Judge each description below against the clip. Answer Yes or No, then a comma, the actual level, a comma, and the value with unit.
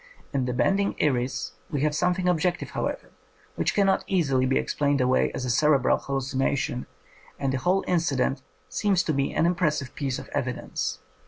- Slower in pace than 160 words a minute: No, average, 175 wpm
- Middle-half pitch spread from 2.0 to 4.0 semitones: No, average, 5.1 semitones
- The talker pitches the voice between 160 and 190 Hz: No, medium, 140 Hz